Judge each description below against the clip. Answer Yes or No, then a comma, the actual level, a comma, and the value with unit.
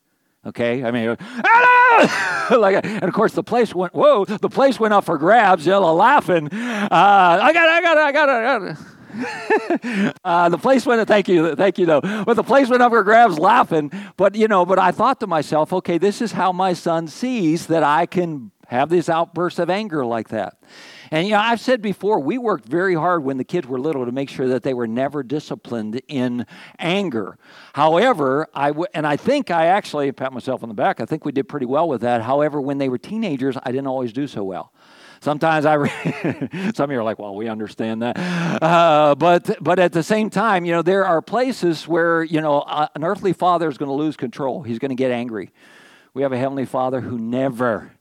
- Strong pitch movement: Yes, wide, 6.7 semitones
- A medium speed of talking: No, fast, 220 wpm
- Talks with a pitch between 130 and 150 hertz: No, medium, 170 Hz